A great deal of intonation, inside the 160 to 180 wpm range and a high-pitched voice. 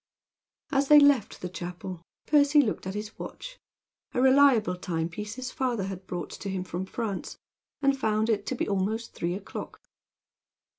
Yes: wide, 5.8 semitones; average, 165 wpm; high, 210 Hz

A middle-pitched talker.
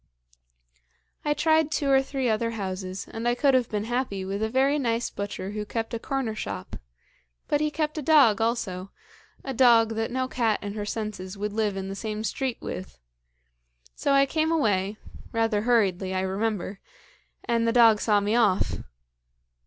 No: high, 225 Hz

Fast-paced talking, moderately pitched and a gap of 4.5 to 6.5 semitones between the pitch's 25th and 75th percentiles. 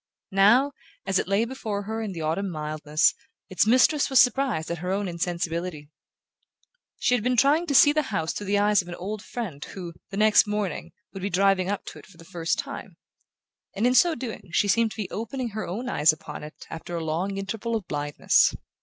No: fast, 215 wpm; high, 200 Hz; average, 5.0 semitones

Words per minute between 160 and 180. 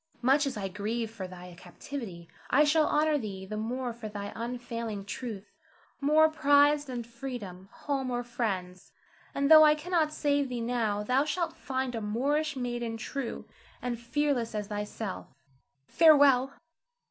No: average, 150 wpm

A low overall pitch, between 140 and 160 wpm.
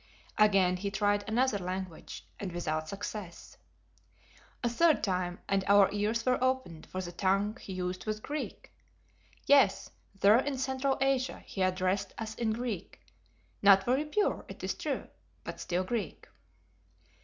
No: high, 205 Hz; average, 145 wpm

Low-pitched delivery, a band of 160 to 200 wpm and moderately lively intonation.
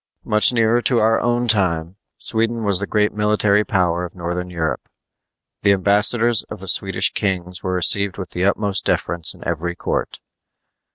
Yes: low, 100 Hz; average, 165 wpm; average, 3.2 semitones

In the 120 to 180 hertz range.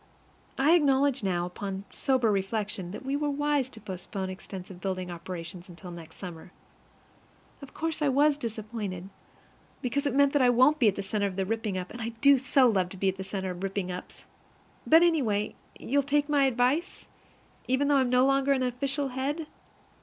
No: high, 235 Hz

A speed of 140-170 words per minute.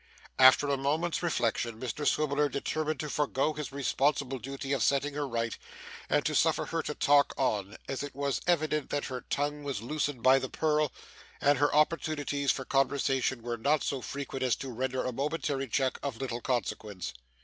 No: average, 180 wpm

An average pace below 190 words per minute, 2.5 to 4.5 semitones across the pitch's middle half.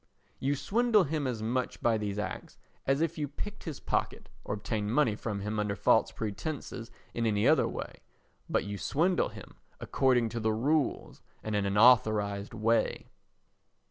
No: average, 170 wpm; average, 5.3 semitones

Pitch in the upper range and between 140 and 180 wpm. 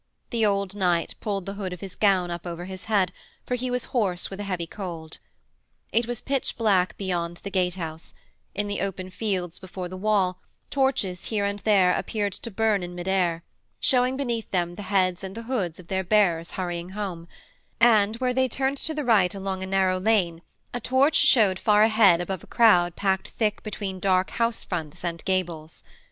No: high, 195 Hz; average, 200 wpm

